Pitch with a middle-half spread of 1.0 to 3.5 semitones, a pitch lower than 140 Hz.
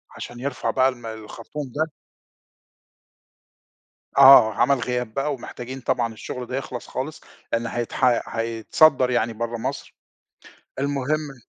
Yes: average, 2.8 semitones; low, 125 Hz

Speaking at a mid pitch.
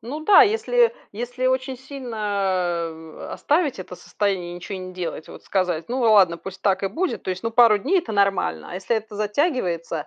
No: high, 205 Hz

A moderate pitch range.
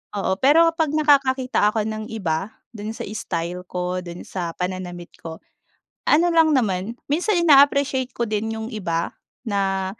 No: wide, 7.1 semitones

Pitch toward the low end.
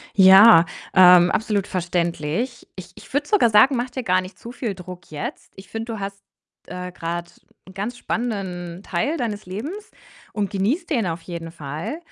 No: high, 195 Hz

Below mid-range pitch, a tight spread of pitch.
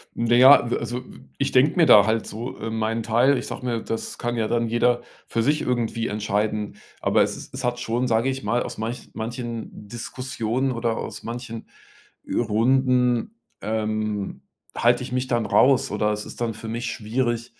Yes: low, 120 Hz; narrow, 2.0 semitones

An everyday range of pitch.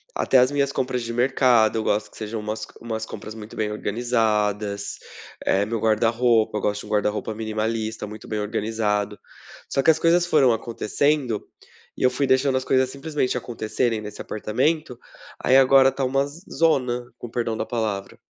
Yes: average, 3.4 semitones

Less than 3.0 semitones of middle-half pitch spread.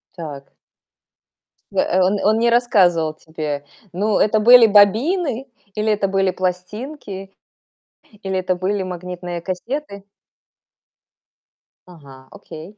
No: average, 3.4 semitones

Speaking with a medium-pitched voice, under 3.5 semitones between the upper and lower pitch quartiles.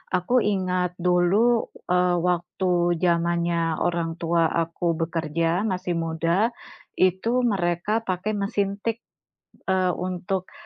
Yes: medium, 180 Hz; narrow, 2.5 semitones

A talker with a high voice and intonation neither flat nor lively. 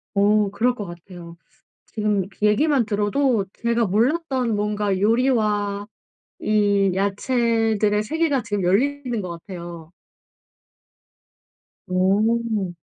Yes: high, 210 Hz; average, 3.0 semitones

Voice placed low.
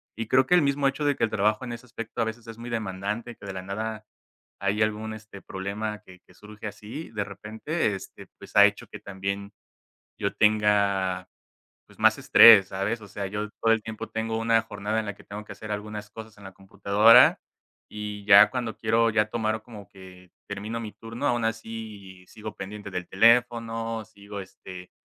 Yes: low, 105 Hz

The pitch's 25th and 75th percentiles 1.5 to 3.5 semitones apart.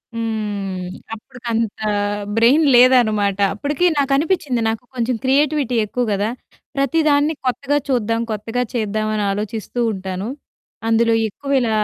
No: average, 4.0 semitones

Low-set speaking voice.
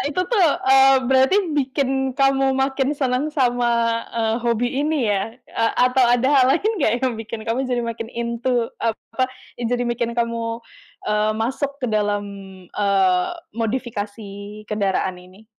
No: high, 240 Hz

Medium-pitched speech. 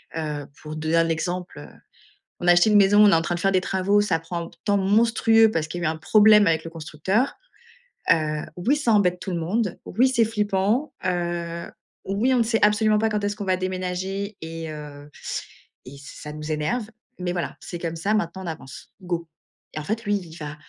Yes: medium, 180 Hz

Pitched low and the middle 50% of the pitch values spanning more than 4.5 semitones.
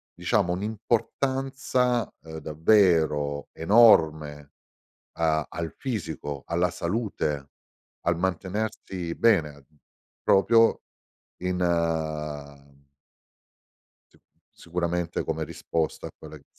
Yes: very low, 85 Hz; wide, 5.5 semitones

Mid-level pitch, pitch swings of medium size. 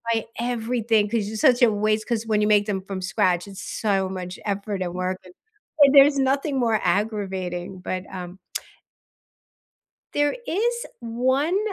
No: high, 215 Hz; average, 4.4 semitones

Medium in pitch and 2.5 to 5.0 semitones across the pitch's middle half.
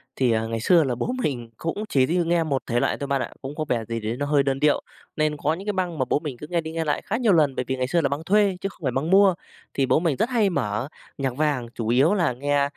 Yes: medium, 145 Hz; average, 4.6 semitones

